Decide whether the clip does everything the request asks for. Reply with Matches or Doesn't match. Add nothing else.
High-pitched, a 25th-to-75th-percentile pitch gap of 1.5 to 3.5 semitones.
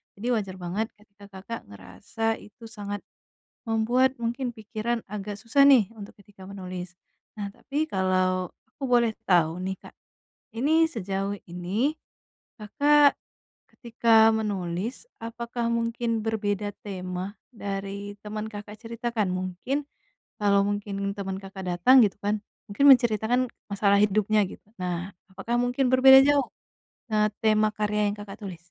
Matches